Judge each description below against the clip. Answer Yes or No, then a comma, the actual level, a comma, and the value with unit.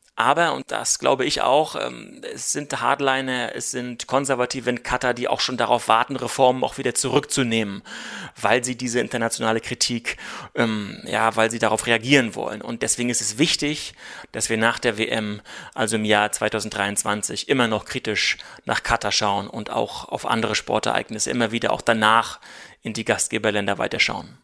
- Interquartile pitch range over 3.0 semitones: No, narrow, 2.4 semitones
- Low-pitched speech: Yes, low, 115 Hz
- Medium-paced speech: Yes, average, 165 wpm